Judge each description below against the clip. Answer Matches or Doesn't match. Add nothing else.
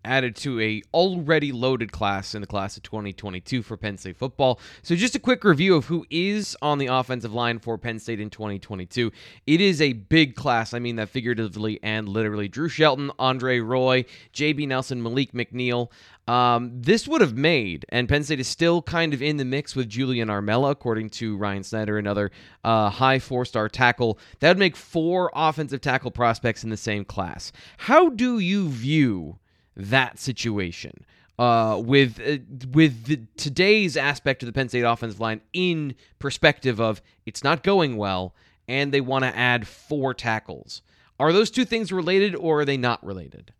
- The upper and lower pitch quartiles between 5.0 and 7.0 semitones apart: Matches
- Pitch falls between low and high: Doesn't match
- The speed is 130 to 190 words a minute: Matches